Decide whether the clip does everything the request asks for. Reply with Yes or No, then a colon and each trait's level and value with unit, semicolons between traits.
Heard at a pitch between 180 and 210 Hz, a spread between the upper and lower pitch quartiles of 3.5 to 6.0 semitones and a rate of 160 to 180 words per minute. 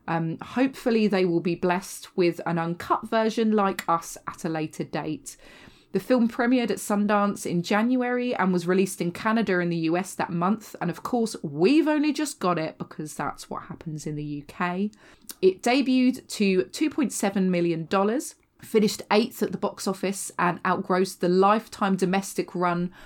Yes: high, 190 Hz; average, 4.0 semitones; average, 170 wpm